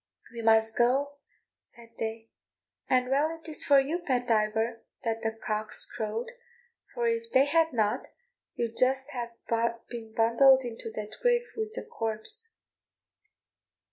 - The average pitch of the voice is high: Yes, high, 245 Hz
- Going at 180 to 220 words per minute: No, average, 140 wpm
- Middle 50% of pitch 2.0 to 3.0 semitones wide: No, average, 4.5 semitones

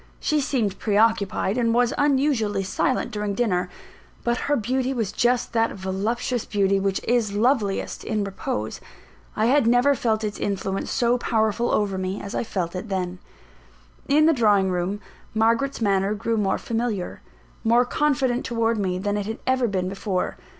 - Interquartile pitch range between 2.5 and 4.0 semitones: Yes, average, 3.7 semitones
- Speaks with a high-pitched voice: Yes, high, 220 Hz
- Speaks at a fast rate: No, average, 165 wpm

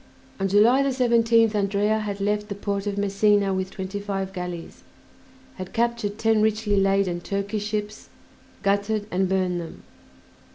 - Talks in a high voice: Yes, high, 205 Hz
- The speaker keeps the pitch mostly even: Yes, narrow, 1.7 semitones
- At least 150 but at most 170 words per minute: No, average, 140 wpm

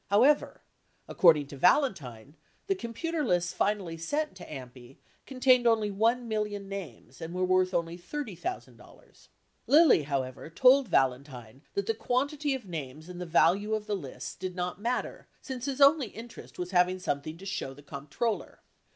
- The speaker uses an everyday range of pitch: No, wide, 7.2 semitones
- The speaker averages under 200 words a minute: Yes, average, 160 wpm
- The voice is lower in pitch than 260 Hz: Yes, high, 190 Hz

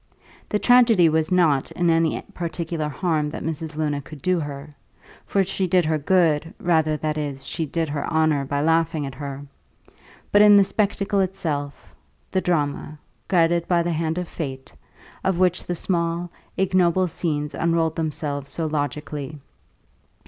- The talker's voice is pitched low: No, medium, 160 Hz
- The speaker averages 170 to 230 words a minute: No, average, 155 wpm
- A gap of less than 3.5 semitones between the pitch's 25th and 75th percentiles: Yes, average, 3.0 semitones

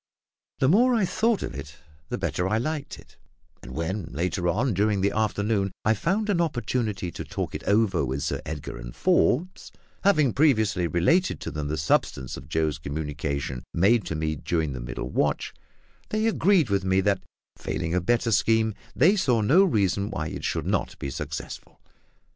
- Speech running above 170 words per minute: Yes, average, 180 wpm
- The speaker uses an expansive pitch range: Yes, wide, 8.5 semitones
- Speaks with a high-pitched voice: No, low, 100 Hz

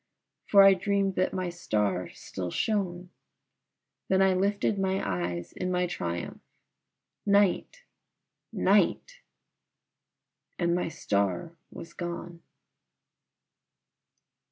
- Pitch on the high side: No, medium, 180 Hz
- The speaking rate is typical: No, slow, 95 wpm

